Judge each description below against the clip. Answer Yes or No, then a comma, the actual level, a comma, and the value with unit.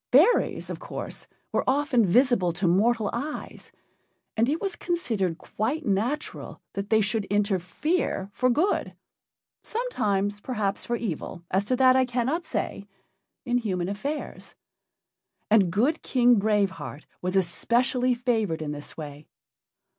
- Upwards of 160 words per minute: No, slow, 135 wpm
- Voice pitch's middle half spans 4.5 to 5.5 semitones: Yes, average, 4.9 semitones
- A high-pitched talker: Yes, high, 225 Hz